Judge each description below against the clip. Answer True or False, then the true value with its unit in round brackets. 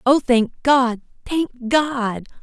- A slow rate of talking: True (125 wpm)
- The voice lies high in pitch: True (250 Hz)